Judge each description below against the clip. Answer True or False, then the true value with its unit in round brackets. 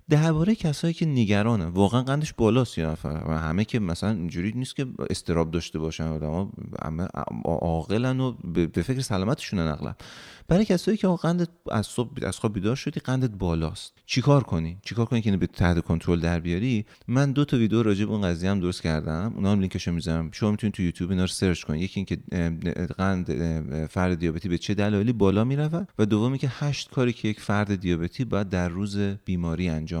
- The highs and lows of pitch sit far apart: True (6.3 semitones)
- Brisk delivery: True (190 wpm)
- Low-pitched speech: True (100 Hz)